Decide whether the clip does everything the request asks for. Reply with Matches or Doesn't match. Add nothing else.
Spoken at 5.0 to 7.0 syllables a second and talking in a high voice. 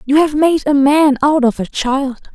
Doesn't match